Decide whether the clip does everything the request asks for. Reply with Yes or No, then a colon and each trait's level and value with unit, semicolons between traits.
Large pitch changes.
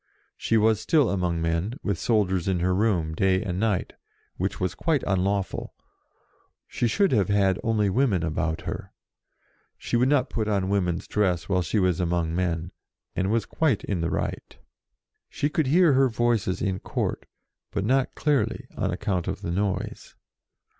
No: average, 4.1 semitones